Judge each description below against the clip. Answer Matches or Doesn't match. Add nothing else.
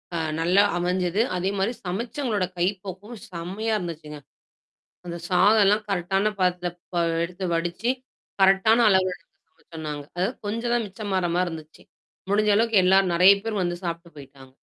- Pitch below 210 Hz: Matches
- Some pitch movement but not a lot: Matches